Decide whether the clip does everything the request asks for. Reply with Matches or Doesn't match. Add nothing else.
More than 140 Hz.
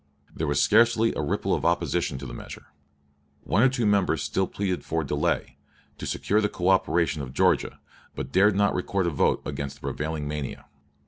Doesn't match